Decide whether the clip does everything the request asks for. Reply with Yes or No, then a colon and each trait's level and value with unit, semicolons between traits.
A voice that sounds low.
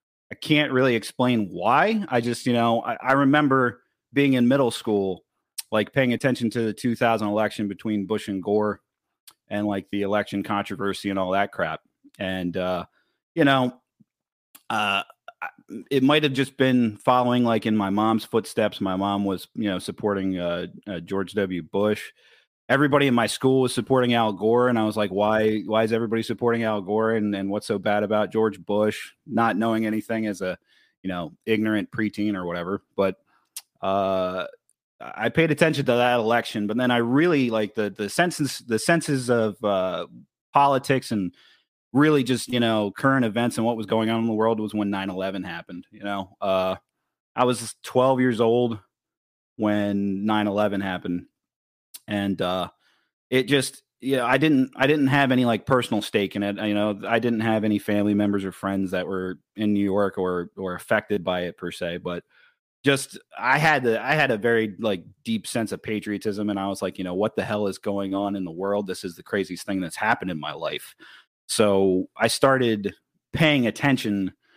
Yes: low, 110 Hz